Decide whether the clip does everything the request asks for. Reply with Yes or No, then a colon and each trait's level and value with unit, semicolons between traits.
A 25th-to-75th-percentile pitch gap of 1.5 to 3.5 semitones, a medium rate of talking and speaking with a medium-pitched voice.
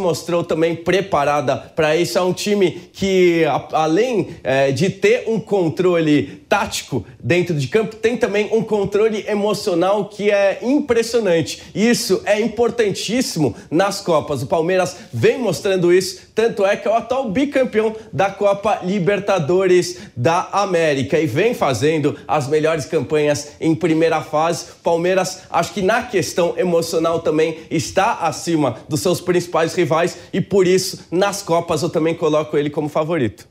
No: average, 4.0 semitones; average, 150 wpm; medium, 175 Hz